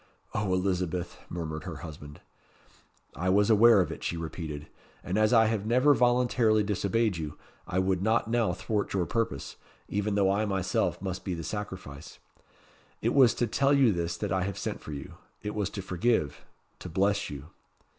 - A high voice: No, low, 100 Hz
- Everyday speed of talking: Yes, average, 180 wpm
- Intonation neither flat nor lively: Yes, average, 4.1 semitones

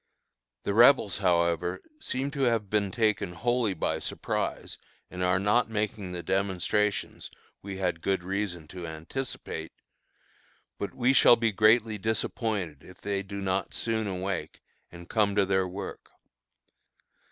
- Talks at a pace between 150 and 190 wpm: No, average, 140 wpm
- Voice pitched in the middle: No, low, 100 Hz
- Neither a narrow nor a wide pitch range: Yes, average, 3.3 semitones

